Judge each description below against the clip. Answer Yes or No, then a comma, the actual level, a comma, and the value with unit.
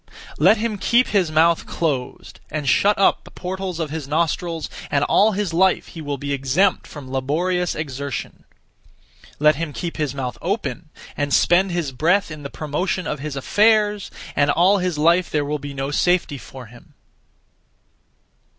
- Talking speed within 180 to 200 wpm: No, average, 170 wpm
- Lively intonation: No, average, 4.4 semitones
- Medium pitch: Yes, medium, 160 Hz